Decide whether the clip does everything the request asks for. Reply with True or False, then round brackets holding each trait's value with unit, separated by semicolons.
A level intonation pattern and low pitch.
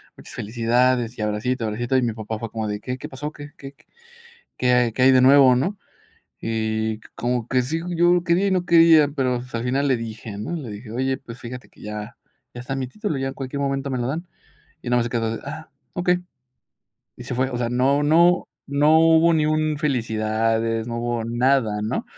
False (3.8 semitones; 125 Hz)